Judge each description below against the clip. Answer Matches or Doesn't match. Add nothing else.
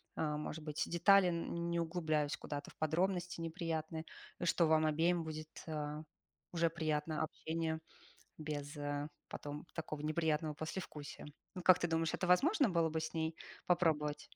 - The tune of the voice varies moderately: Doesn't match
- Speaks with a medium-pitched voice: Matches